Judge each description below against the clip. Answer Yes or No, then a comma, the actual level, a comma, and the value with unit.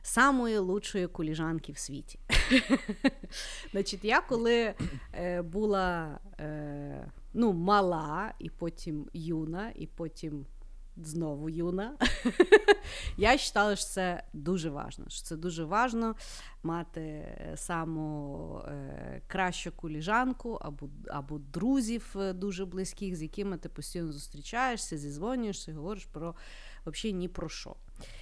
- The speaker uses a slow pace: Yes, slow, 100 wpm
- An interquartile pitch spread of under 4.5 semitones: No, average, 5.0 semitones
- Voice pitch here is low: No, medium, 175 Hz